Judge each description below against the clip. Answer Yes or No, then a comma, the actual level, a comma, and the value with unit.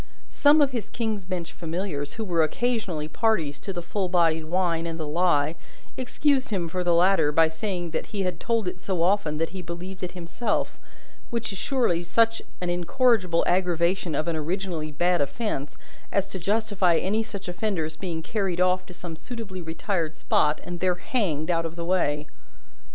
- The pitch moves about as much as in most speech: Yes, average, 3.5 semitones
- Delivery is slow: No, average, 185 wpm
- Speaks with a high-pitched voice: No, medium, 180 Hz